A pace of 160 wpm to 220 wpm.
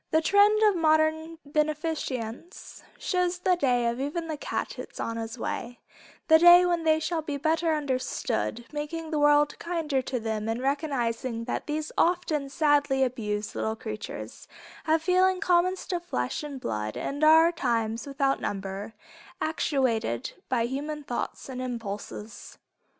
No: average, 150 wpm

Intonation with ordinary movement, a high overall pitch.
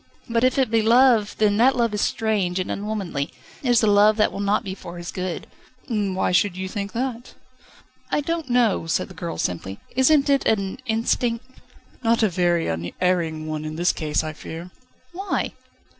Yes: average, 4.9 semitones; high, 205 Hz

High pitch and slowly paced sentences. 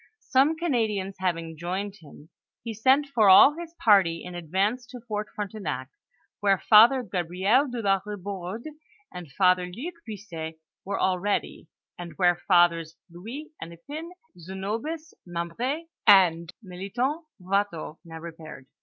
Yes: high, 195 Hz; slow, 130 wpm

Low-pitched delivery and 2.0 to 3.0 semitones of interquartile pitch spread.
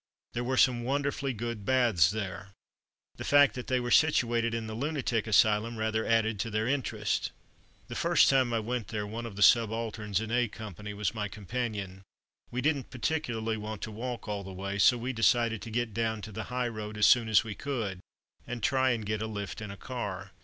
Yes: low, 115 Hz; narrow, 2.6 semitones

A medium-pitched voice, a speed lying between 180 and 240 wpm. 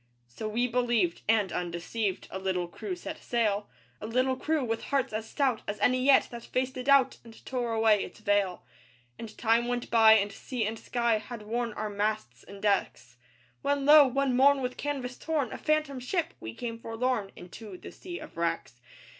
No: high, 230 Hz; average, 190 wpm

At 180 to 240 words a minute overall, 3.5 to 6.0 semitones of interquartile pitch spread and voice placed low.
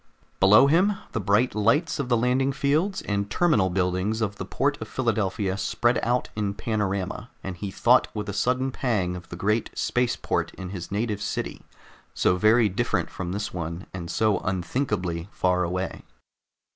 No: average, 170 wpm; average, 4.7 semitones; low, 105 Hz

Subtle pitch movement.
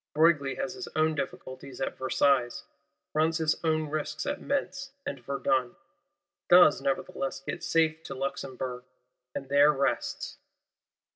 No: average, 3.1 semitones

